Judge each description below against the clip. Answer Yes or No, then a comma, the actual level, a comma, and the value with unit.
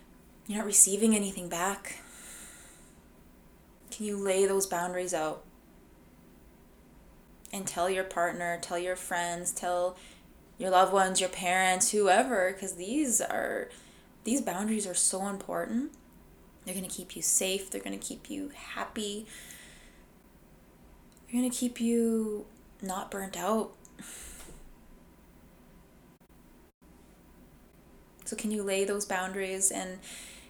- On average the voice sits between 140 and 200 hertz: Yes, high, 190 Hz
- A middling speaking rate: No, slow, 120 wpm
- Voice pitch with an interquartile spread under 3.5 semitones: Yes, average, 2.8 semitones